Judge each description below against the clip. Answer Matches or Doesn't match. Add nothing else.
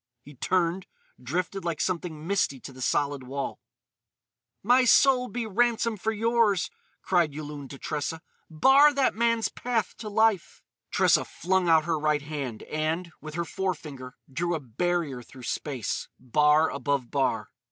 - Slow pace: Doesn't match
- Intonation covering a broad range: Matches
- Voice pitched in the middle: Matches